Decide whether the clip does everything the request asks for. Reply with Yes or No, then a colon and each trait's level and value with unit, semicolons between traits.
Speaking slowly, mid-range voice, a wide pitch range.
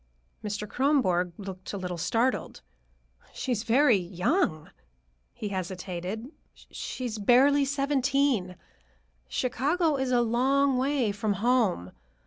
No: slow, 115 wpm; high, 235 Hz; wide, 6.0 semitones